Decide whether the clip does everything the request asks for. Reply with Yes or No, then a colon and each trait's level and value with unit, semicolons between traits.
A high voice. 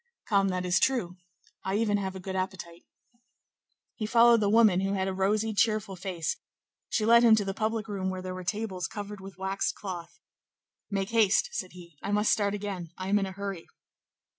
Yes: high, 195 Hz